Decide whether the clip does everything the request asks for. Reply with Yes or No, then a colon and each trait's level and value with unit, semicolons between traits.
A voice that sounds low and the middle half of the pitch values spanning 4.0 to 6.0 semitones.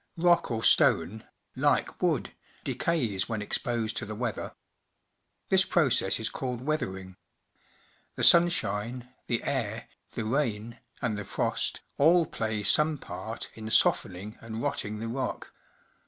Yes: low, 115 Hz; average, 4.3 semitones